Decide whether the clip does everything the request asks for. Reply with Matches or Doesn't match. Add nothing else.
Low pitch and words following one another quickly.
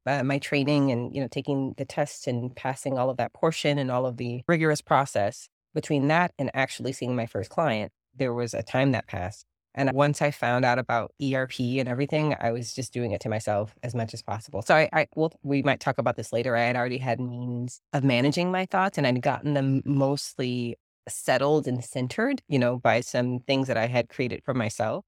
Matches